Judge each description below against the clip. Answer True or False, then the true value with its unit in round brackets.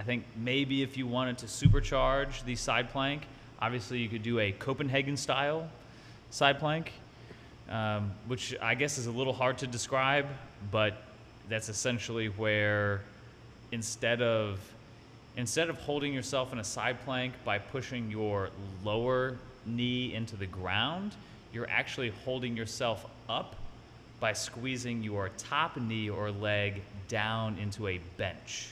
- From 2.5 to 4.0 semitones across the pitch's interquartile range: True (3.3 semitones)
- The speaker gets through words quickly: False (140 wpm)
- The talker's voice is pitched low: True (120 Hz)